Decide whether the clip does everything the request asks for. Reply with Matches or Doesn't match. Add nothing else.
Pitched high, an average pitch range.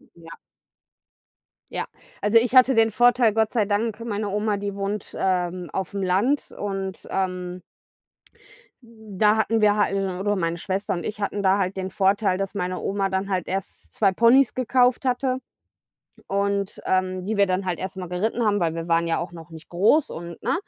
Matches